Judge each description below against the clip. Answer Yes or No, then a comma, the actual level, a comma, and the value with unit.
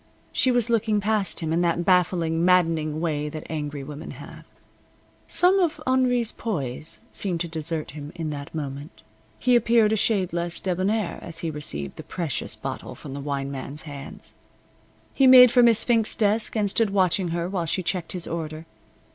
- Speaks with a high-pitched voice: No, medium, 170 Hz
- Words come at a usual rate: Yes, average, 180 wpm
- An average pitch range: No, wide, 5.7 semitones